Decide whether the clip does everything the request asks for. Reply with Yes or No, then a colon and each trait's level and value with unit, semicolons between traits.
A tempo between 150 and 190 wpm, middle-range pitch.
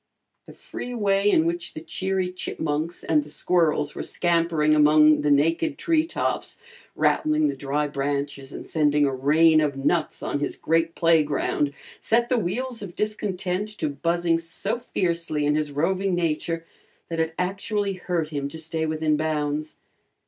Yes: average, 160 wpm; medium, 165 Hz